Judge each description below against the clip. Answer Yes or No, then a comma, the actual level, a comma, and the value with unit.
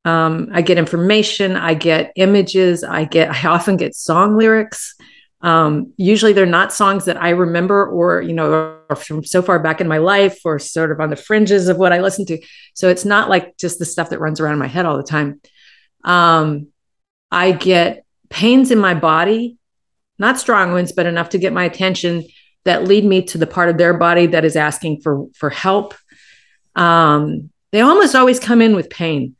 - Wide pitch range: No, average, 3.5 semitones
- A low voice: No, medium, 175 Hz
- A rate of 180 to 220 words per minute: Yes, average, 200 wpm